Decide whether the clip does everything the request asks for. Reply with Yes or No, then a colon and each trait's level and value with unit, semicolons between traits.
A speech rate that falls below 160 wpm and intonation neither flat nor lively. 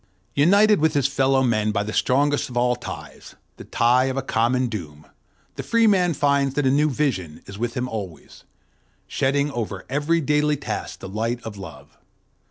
No: average, 180 wpm; average, 4.5 semitones